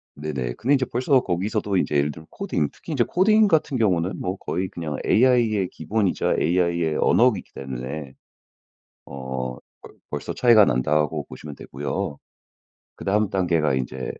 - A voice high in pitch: No, very low, 85 Hz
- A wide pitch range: Yes, wide, 7.1 semitones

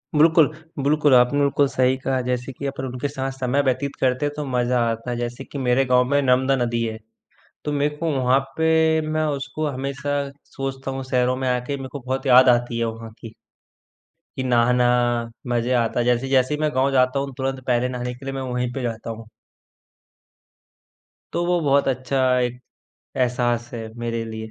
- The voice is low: Yes, low, 130 Hz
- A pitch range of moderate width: No, narrow, 2.1 semitones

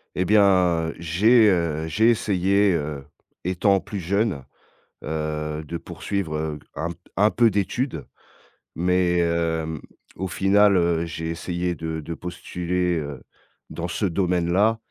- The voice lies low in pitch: Yes, very low, 85 Hz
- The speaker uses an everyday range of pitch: Yes, average, 3.3 semitones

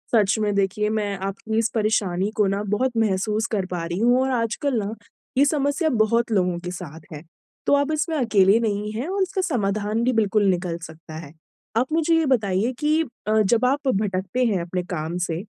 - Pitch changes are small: No, average, 4.7 semitones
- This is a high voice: Yes, high, 215 Hz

